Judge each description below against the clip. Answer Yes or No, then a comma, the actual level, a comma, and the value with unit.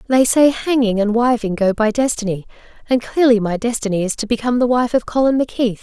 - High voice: Yes, high, 235 Hz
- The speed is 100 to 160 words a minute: No, fast, 205 wpm